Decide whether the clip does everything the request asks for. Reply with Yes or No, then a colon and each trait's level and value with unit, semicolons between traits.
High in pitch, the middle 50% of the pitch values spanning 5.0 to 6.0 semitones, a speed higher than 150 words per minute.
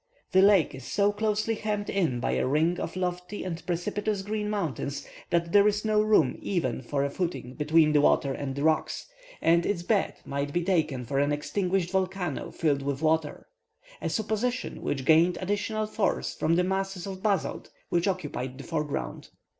No: medium, 175 Hz; wide, 5.4 semitones; average, 180 wpm